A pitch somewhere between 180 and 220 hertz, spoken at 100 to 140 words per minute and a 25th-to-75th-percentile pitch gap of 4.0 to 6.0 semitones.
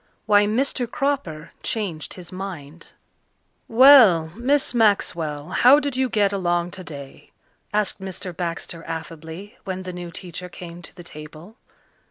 Yes: medium, 185 Hz; slow, 135 wpm; average, 4.6 semitones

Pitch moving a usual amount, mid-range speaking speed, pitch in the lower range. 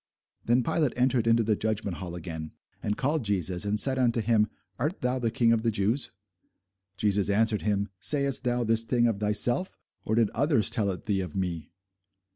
Yes: average, 3.3 semitones; average, 190 wpm; low, 110 Hz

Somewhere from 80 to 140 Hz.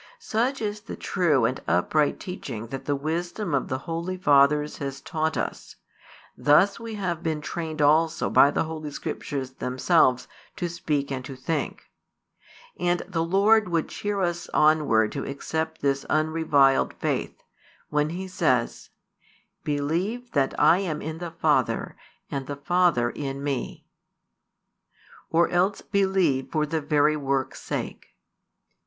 No: medium, 155 Hz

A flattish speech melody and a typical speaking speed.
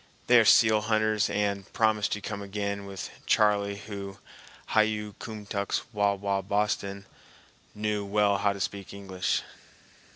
No: narrow, 1.1 semitones; slow, 130 wpm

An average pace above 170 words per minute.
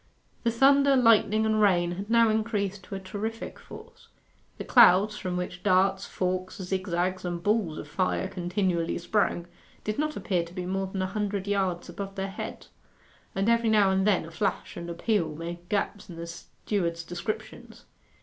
Yes: average, 180 wpm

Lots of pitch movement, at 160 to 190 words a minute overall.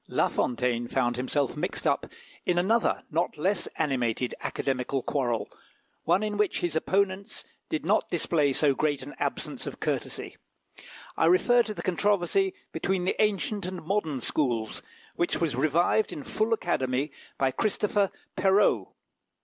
No: wide, 6.8 semitones; average, 145 wpm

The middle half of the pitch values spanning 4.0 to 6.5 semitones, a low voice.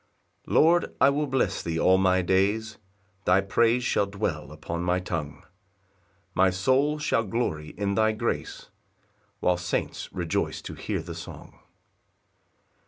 Yes: average, 4.3 semitones; very low, 95 Hz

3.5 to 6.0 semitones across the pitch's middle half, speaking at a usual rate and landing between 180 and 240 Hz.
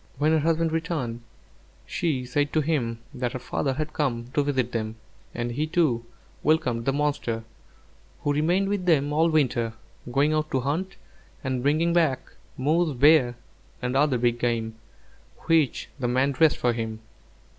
No: average, 4.3 semitones; average, 160 wpm; medium, 140 Hz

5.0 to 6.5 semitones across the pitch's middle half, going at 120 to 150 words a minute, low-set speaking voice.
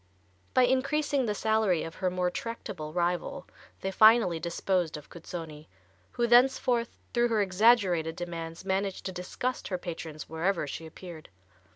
No: wide, 5.6 semitones; average, 145 wpm; medium, 185 Hz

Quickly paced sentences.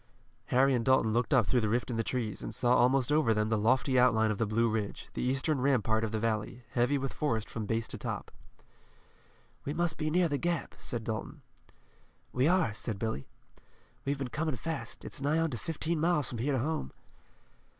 Yes: fast, 210 wpm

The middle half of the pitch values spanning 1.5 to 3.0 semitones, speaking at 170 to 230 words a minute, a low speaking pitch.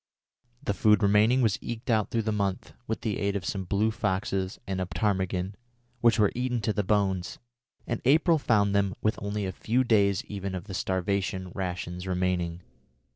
Yes: average, 2.7 semitones; average, 180 wpm; low, 100 Hz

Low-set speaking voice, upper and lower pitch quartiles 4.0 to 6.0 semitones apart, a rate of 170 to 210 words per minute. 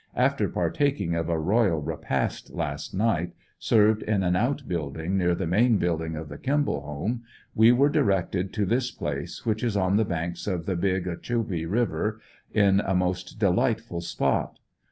Yes: very low, 95 Hz; average, 4.6 semitones; average, 175 wpm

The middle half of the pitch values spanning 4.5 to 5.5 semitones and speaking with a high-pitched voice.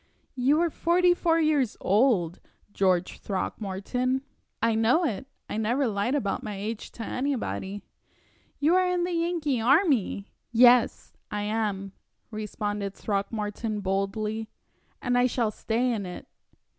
Yes: average, 5.0 semitones; high, 225 Hz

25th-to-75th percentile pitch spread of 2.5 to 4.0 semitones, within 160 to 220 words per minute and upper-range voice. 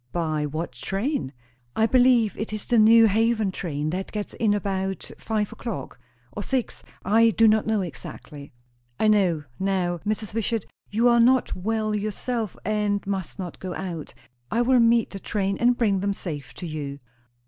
Yes: average, 3.5 semitones; average, 170 wpm; high, 205 Hz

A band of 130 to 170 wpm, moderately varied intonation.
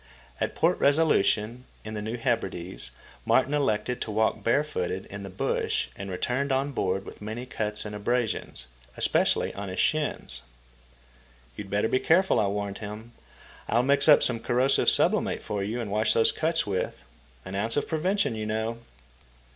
Yes: average, 165 wpm; average, 4.6 semitones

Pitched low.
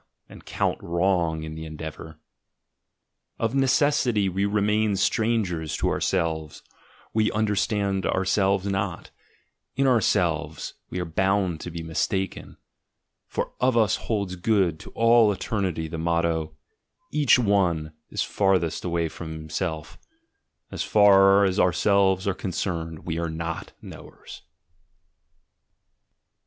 Yes: very low, 95 Hz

